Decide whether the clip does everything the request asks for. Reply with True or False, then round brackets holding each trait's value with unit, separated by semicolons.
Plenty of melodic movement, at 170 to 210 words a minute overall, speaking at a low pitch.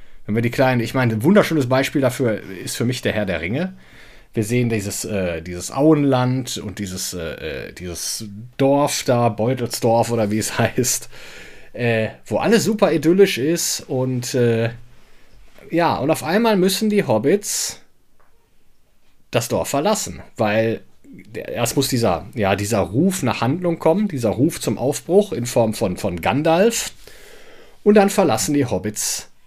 False (6.3 semitones; 150 wpm; 125 Hz)